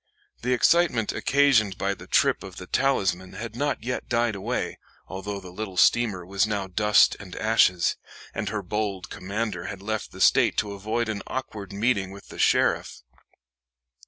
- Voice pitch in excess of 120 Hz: No, low, 105 Hz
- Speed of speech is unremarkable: Yes, average, 165 wpm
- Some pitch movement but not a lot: Yes, average, 3.2 semitones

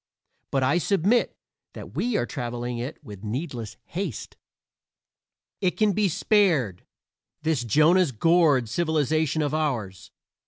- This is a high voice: No, medium, 150 Hz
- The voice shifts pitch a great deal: Yes, wide, 6.2 semitones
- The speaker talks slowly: Yes, slow, 120 wpm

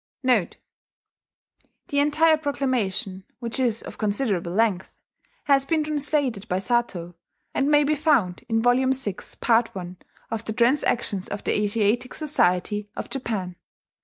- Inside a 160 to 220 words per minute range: No, slow, 135 wpm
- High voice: Yes, high, 235 Hz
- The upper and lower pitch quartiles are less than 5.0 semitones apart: No, wide, 5.4 semitones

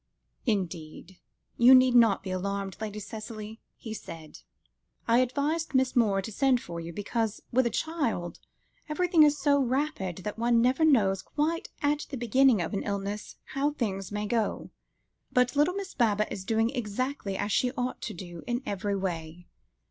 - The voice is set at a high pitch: Yes, high, 225 Hz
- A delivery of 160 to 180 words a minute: Yes, average, 170 wpm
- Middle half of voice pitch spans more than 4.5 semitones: Yes, average, 4.9 semitones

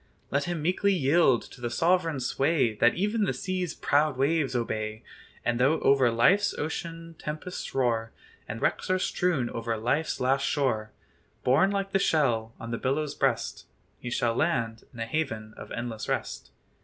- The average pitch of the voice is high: No, low, 135 Hz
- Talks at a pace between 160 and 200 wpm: Yes, average, 165 wpm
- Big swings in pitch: Yes, wide, 6.0 semitones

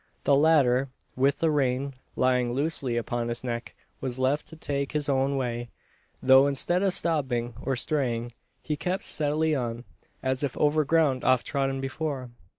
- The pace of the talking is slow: No, average, 160 wpm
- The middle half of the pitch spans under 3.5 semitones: Yes, average, 3.0 semitones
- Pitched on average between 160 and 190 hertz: No, low, 135 Hz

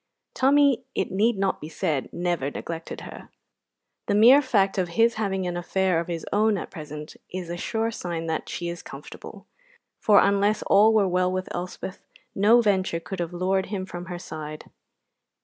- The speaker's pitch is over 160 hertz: Yes, medium, 185 Hz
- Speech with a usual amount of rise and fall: Yes, average, 3.2 semitones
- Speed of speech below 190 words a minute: Yes, average, 180 wpm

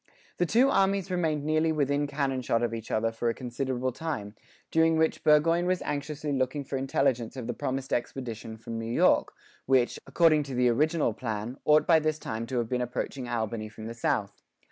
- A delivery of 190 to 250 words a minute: Yes, average, 195 wpm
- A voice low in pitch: Yes, low, 130 Hz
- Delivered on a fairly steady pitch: No, average, 4.8 semitones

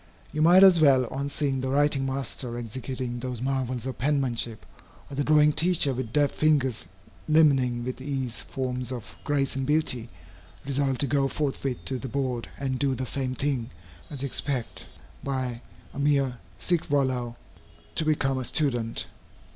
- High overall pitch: No, low, 135 Hz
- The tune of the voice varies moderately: No, narrow, 2.3 semitones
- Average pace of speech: Yes, average, 160 wpm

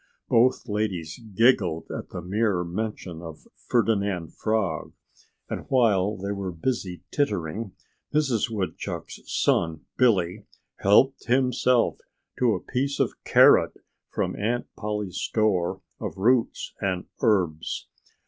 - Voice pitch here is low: Yes, low, 105 Hz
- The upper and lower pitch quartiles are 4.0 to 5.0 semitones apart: Yes, average, 4.5 semitones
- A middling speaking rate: No, slow, 115 wpm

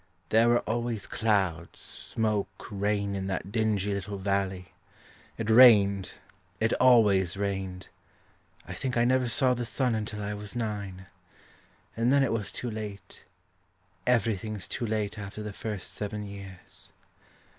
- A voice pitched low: Yes, low, 105 Hz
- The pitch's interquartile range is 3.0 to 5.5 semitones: No, narrow, 2.5 semitones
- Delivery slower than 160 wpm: Yes, average, 140 wpm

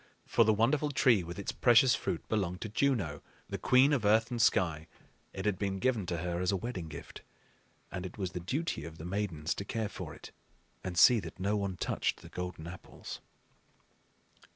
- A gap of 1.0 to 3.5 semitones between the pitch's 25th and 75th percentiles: No, average, 4.4 semitones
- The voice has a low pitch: Yes, low, 100 Hz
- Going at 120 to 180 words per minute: No, average, 200 wpm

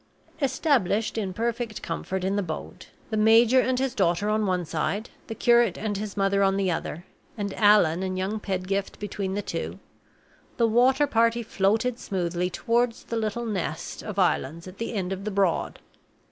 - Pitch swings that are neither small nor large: Yes, average, 3.4 semitones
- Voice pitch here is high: Yes, high, 205 Hz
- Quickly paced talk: No, average, 175 wpm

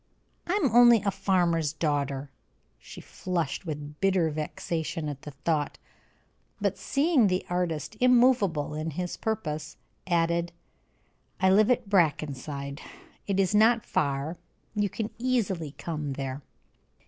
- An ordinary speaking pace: No, slow, 125 wpm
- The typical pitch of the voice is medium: Yes, medium, 170 Hz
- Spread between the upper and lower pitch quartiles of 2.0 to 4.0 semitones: No, wide, 5.6 semitones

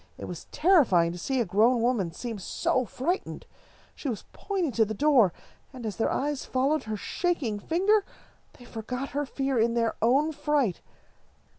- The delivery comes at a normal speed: Yes, average, 170 wpm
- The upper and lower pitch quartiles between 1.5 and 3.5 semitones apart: No, average, 5.0 semitones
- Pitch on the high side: Yes, very high, 250 Hz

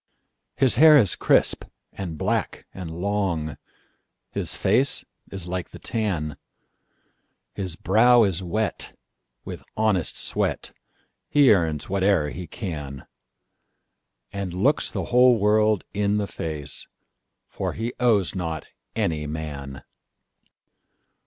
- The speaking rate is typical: No, slow, 100 wpm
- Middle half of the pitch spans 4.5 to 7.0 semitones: Yes, average, 5.2 semitones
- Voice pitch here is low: Yes, very low, 95 Hz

